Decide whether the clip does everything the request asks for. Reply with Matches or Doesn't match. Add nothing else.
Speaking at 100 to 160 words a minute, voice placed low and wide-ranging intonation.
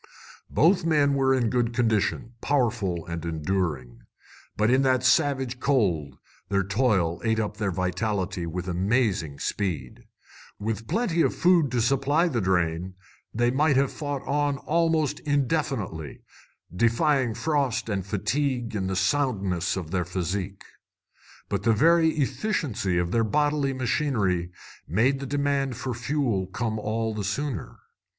Matches